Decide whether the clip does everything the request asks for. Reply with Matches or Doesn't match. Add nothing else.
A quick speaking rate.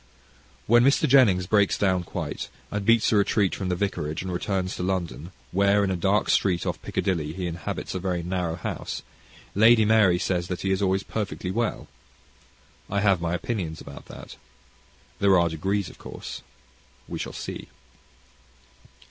Doesn't match